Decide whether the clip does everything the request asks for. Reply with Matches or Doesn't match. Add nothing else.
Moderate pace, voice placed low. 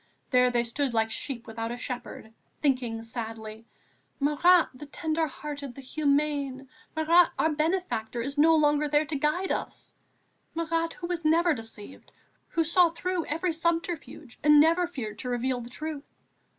Doesn't match